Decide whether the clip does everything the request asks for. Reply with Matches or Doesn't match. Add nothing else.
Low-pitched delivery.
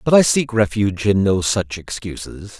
Matches